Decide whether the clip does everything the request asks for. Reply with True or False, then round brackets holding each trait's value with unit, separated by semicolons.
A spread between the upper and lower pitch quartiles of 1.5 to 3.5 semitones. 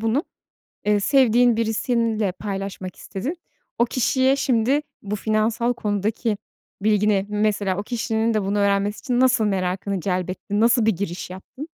True (3.0 semitones)